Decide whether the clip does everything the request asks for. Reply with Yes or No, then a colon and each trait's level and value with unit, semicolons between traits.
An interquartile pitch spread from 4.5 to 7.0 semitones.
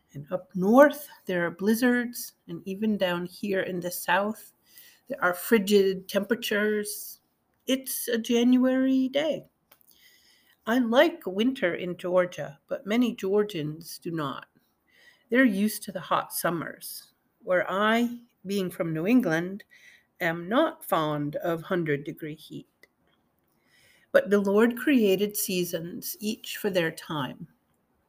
Yes: average, 5.2 semitones